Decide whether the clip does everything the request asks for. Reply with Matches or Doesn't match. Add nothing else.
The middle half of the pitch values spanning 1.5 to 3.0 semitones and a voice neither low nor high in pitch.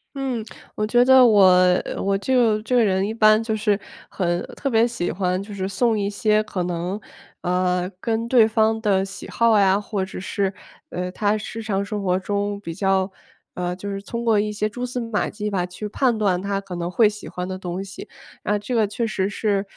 Doesn't match